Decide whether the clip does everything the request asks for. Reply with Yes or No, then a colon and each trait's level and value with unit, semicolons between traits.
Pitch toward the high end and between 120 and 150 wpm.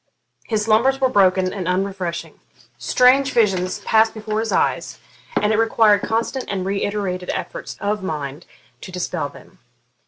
Yes: high, 205 Hz; average, 145 wpm